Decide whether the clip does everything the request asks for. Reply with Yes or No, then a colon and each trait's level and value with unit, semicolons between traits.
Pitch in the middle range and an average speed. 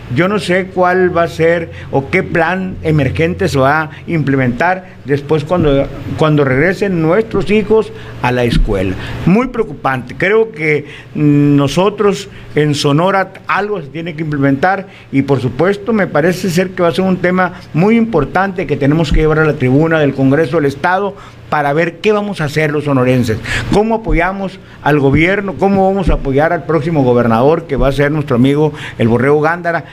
Yes: medium, 160 Hz; average, 180 wpm